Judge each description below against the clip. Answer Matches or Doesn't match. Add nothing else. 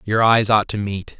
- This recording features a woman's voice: Doesn't match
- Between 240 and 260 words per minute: Matches